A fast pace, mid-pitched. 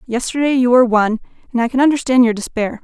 No: fast, 210 wpm; high, 245 Hz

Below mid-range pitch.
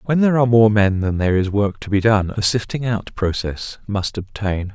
Yes: low, 105 Hz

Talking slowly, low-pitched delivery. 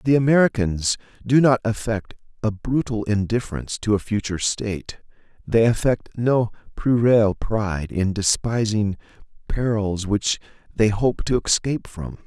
Yes: slow, 125 wpm; low, 110 Hz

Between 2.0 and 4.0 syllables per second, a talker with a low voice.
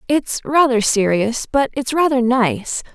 No: 3.9 syllables/s; high, 245 Hz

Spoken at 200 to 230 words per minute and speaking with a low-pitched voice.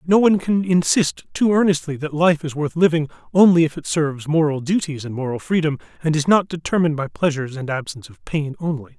No: fast, 205 wpm; medium, 160 Hz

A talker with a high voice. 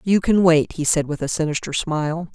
No: medium, 165 Hz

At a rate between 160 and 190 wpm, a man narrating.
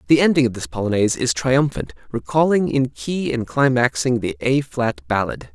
Yes: average, 175 wpm; male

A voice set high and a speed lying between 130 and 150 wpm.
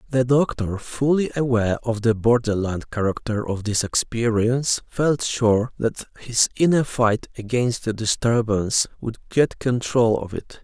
No: low, 115 Hz; average, 140 wpm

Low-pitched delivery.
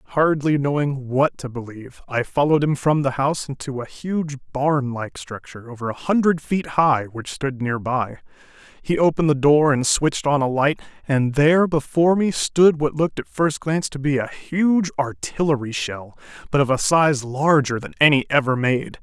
No: medium, 145 Hz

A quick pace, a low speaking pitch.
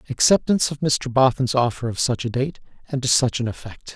Yes: fast, 210 wpm; low, 130 Hz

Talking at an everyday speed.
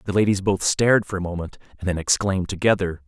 No: fast, 215 wpm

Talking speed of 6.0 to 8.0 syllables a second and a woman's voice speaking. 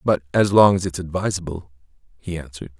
No: 6.2 syllables/s; male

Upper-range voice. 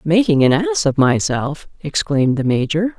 No: medium, 165 Hz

